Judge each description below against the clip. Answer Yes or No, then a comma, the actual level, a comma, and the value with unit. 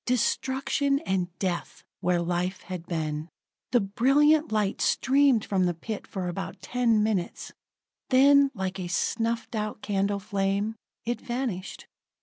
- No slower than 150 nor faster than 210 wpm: No, slow, 135 wpm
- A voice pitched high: Yes, high, 210 Hz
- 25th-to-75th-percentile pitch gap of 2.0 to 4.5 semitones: No, average, 5.1 semitones